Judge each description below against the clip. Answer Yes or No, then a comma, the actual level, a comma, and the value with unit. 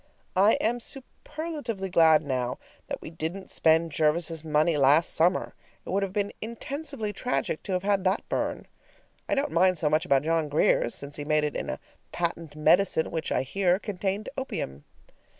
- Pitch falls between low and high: Yes, medium, 170 Hz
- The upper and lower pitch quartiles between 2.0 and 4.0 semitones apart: No, average, 4.6 semitones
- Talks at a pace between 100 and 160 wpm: No, average, 175 wpm